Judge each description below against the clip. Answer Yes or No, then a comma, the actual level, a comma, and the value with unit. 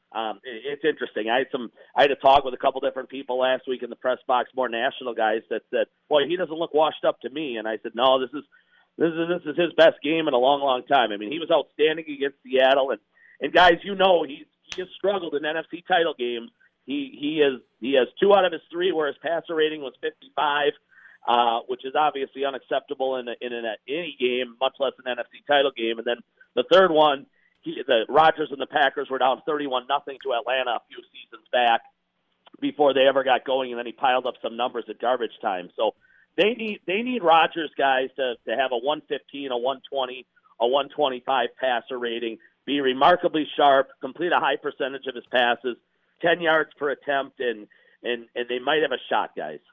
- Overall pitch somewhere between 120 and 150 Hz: Yes, medium, 140 Hz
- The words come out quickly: Yes, fast, 225 wpm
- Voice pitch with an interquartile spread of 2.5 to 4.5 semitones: No, average, 5.2 semitones